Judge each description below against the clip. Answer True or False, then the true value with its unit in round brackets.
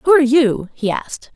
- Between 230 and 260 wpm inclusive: False (220 wpm)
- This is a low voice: False (265 Hz)